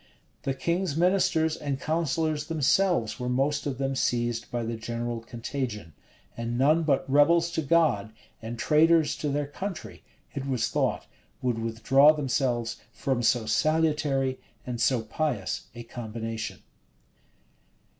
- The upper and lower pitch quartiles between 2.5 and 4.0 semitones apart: No, average, 4.7 semitones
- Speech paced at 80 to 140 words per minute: Yes, slow, 135 wpm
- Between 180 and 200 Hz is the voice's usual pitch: No, low, 135 Hz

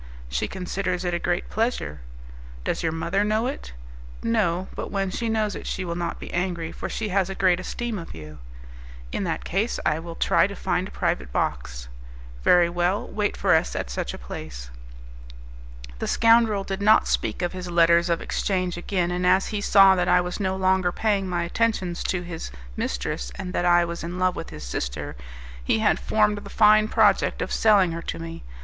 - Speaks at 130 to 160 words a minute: No, average, 200 wpm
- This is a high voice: No, medium, 180 Hz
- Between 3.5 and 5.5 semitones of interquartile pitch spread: No, average, 3.0 semitones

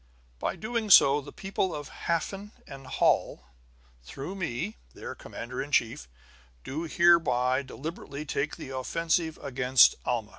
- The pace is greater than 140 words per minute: No, slow, 135 wpm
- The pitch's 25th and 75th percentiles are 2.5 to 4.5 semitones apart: No, average, 4.9 semitones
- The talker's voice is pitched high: No, medium, 140 Hz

